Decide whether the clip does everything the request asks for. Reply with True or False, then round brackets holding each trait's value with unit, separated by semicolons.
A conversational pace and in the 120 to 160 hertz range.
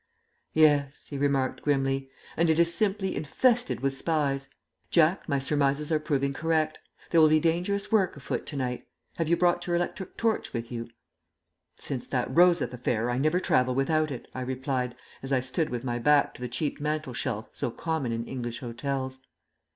True (180 wpm; 140 Hz)